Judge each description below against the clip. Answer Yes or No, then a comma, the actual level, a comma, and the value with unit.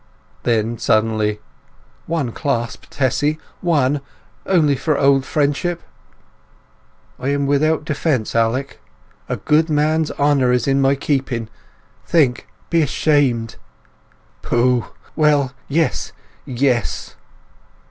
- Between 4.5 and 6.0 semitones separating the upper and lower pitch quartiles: No, average, 3.6 semitones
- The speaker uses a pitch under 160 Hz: Yes, medium, 140 Hz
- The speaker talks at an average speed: No, slow, 85 wpm